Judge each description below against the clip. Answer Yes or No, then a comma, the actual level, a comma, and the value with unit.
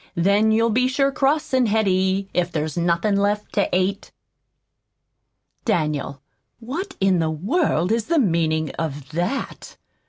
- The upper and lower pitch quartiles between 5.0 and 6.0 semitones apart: Yes, wide, 5.4 semitones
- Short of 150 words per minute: Yes, slow, 135 wpm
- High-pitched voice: Yes, high, 195 Hz